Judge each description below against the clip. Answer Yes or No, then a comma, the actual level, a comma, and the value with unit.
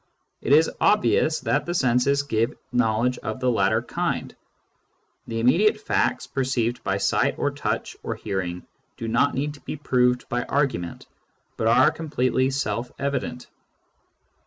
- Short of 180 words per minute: Yes, average, 150 wpm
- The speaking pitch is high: No, low, 125 Hz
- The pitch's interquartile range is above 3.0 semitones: Yes, average, 3.7 semitones